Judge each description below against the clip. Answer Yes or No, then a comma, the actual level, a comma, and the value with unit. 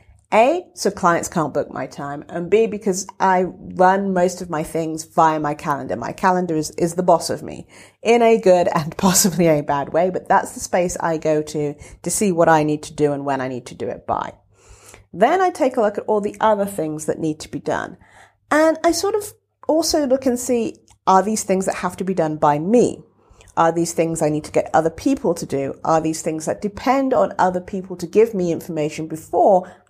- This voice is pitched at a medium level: Yes, medium, 175 Hz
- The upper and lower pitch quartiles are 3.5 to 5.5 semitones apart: Yes, average, 4.8 semitones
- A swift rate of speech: Yes, fast, 230 wpm